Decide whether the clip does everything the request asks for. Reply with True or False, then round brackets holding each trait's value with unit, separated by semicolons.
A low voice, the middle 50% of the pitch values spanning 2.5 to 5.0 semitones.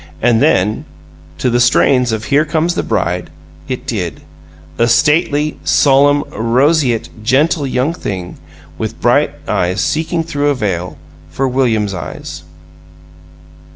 False (130 Hz; 5.5 semitones)